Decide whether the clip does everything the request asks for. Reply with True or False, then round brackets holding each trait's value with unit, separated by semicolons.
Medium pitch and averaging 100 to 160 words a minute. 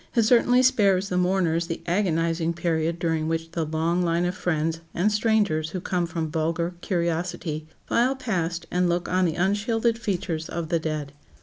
False (170 Hz; 175 wpm)